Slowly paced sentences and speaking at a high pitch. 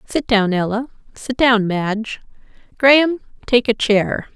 Yes: slow, 110 wpm; high, 230 Hz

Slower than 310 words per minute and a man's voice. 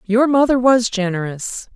No: slow, 135 wpm; female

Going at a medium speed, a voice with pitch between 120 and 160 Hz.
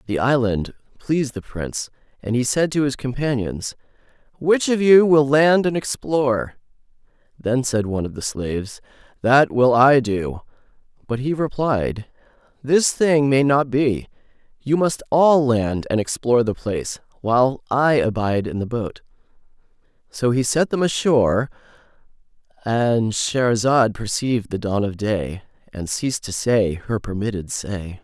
Yes: average, 150 wpm; low, 125 Hz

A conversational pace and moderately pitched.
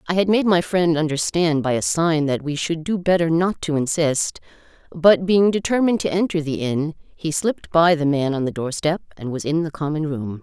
No: fast, 220 wpm; medium, 160 Hz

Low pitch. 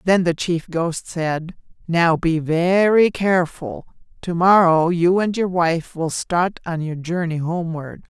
No: medium, 170 Hz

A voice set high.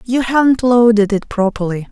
Yes: high, 225 Hz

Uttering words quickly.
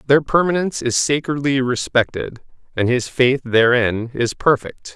No: slow, 135 wpm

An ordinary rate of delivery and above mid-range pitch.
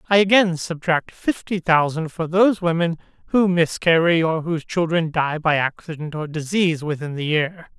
No: average, 160 wpm; medium, 165 Hz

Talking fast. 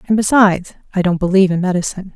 No: average, 195 wpm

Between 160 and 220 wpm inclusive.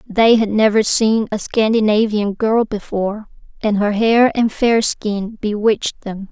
No: average, 150 wpm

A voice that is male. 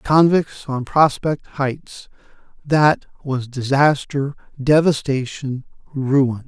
Yes: male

